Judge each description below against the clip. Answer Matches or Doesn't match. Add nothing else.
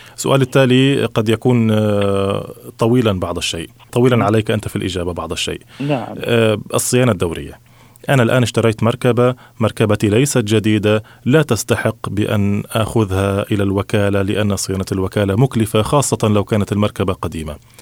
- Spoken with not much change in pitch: Doesn't match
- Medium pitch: Doesn't match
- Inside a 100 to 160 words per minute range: Matches